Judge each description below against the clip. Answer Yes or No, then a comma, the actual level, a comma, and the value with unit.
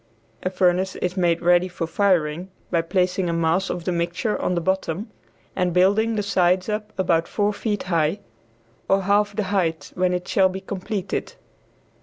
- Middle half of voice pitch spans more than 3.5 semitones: No, narrow, 2.5 semitones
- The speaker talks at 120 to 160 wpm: No, average, 175 wpm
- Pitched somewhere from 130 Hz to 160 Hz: No, medium, 185 Hz